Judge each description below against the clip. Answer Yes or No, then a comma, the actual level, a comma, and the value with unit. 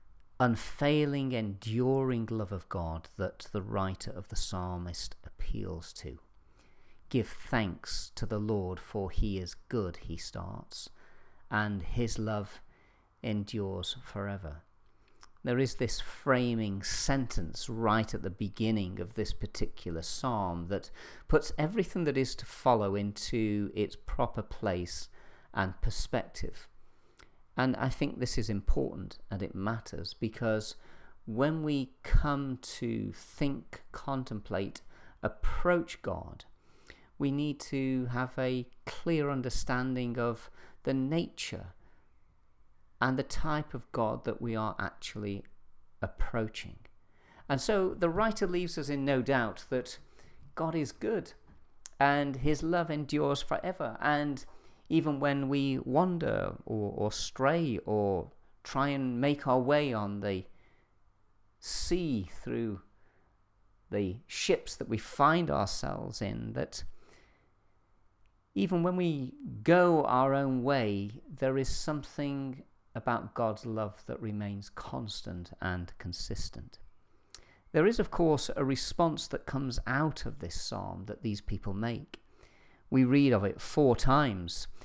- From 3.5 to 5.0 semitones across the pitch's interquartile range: No, wide, 5.5 semitones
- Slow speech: Yes, slow, 125 wpm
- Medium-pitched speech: No, low, 110 Hz